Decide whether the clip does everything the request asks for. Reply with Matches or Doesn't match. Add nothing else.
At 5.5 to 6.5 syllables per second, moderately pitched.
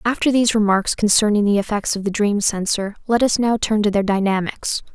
Doesn't match